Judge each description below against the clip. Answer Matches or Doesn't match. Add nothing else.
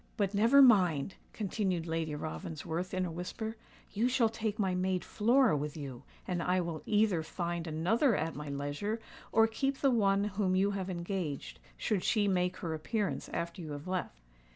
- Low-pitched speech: Doesn't match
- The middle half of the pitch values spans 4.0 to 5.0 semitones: Matches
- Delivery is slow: Doesn't match